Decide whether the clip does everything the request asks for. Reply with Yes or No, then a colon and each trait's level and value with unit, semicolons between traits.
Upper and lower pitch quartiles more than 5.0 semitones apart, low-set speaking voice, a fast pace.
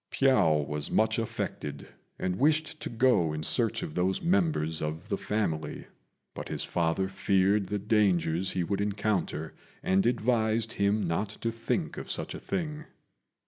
No: wide, 5.4 semitones; low, 100 Hz; average, 155 wpm